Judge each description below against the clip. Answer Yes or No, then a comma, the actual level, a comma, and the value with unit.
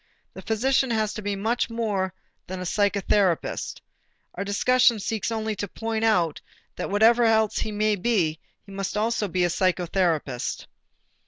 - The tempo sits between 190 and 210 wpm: No, average, 155 wpm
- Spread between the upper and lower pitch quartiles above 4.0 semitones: No, average, 3.1 semitones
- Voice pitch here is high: Yes, high, 205 Hz